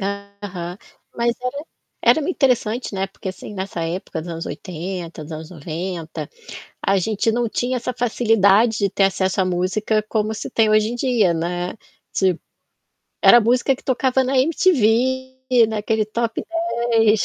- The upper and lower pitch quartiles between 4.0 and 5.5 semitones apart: Yes, average, 4.5 semitones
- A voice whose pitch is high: Yes, high, 215 Hz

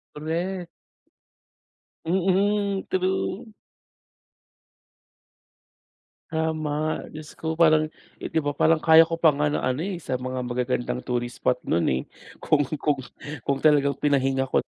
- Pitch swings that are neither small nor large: Yes, average, 3.7 semitones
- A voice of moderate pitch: Yes, medium, 155 Hz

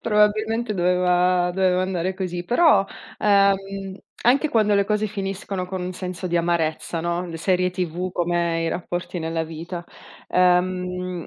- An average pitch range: No, narrow, 2.0 semitones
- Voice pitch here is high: No, medium, 180 Hz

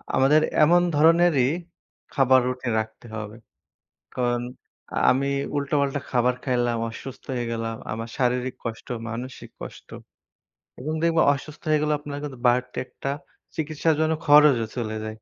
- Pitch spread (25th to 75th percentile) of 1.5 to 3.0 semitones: No, average, 3.5 semitones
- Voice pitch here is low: Yes, low, 130 Hz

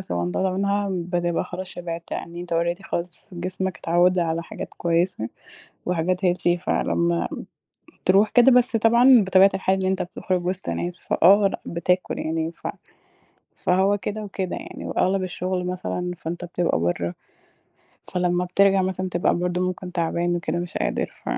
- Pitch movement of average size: No, narrow, 1.7 semitones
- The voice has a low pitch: No, medium, 180 Hz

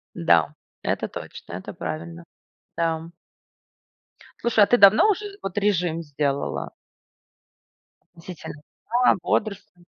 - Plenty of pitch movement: Yes, wide, 6.1 semitones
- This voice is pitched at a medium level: Yes, medium, 175 Hz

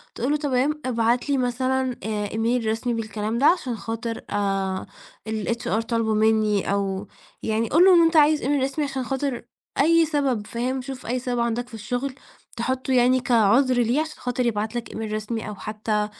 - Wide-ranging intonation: No, average, 3.2 semitones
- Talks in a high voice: Yes, high, 240 Hz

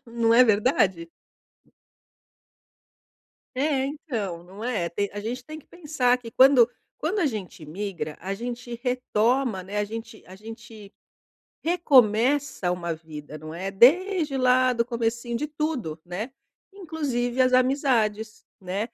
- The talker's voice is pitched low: No, high, 235 Hz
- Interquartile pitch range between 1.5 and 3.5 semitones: No, average, 4.7 semitones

